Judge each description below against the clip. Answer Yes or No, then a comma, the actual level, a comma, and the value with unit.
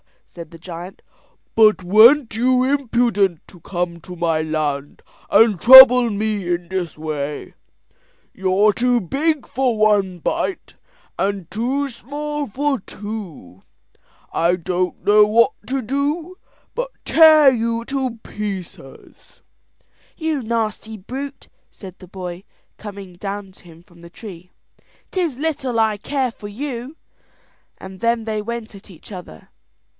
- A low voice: No, high, 215 Hz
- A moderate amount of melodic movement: No, wide, 6.0 semitones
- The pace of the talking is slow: Yes, slow, 130 wpm